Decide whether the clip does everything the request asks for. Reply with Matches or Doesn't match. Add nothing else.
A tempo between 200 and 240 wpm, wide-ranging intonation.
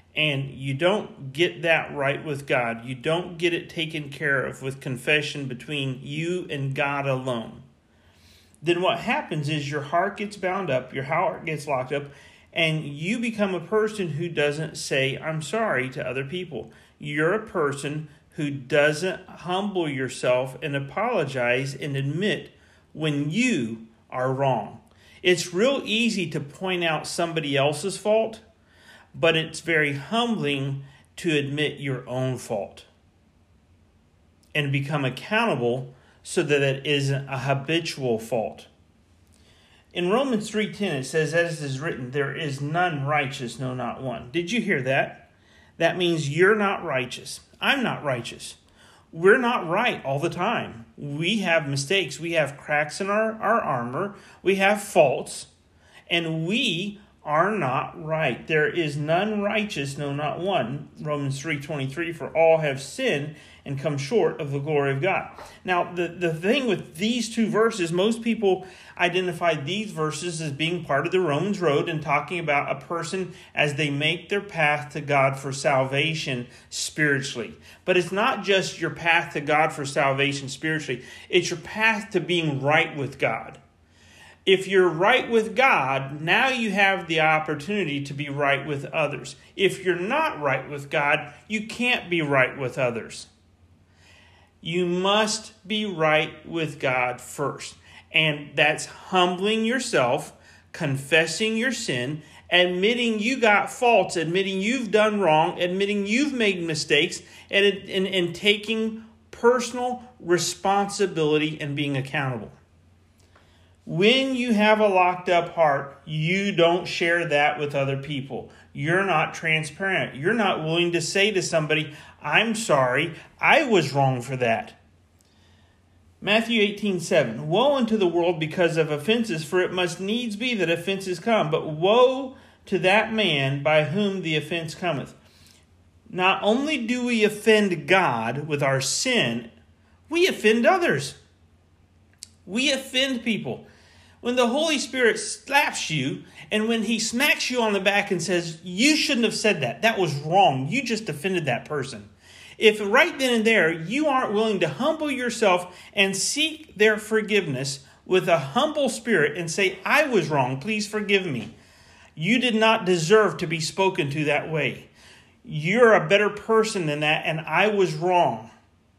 Doesn't match